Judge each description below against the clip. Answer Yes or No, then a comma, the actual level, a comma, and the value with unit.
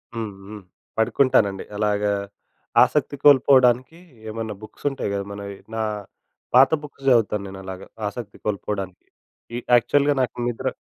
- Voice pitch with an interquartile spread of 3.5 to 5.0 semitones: Yes, average, 4.0 semitones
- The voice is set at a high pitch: No, low, 110 Hz